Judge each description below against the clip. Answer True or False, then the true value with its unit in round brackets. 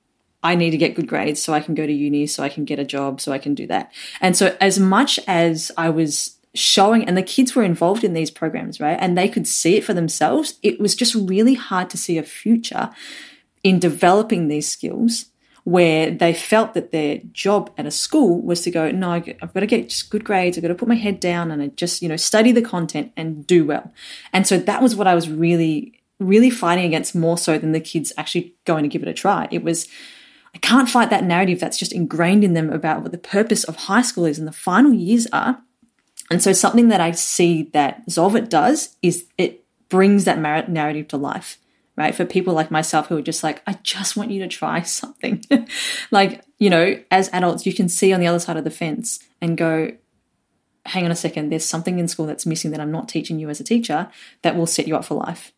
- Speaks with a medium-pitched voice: True (175 Hz)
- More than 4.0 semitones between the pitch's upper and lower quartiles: True (4.4 semitones)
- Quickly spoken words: True (235 wpm)